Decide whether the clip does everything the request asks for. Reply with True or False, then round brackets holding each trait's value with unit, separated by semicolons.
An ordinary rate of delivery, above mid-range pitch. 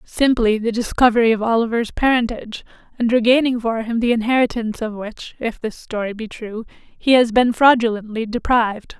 True (160 wpm; 230 Hz)